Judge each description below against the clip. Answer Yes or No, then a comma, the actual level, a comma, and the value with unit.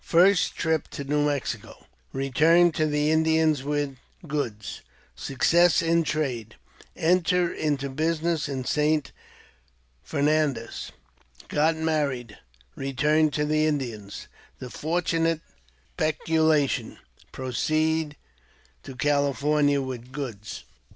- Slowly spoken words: Yes, slow, 120 wpm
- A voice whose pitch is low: No, medium, 150 Hz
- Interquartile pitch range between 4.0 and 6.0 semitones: No, average, 2.9 semitones